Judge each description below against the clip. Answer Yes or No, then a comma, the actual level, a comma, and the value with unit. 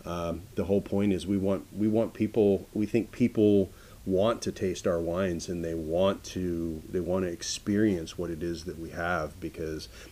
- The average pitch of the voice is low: Yes, very low, 95 Hz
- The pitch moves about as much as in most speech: Yes, average, 3.4 semitones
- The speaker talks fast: No, average, 195 wpm